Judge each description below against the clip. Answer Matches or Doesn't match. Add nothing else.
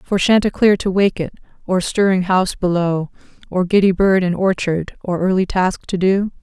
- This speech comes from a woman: Matches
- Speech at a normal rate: Matches